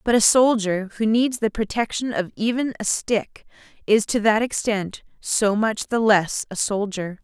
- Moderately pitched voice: No, high, 215 Hz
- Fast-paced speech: No, average, 175 wpm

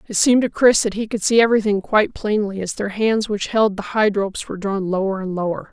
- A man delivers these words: No, female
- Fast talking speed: Yes, fast, 250 wpm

